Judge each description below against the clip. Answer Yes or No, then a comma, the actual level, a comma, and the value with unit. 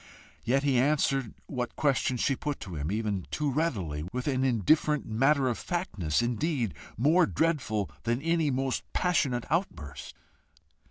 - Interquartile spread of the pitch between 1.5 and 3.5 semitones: No, average, 5.1 semitones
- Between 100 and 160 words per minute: Yes, average, 145 wpm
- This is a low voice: Yes, low, 130 Hz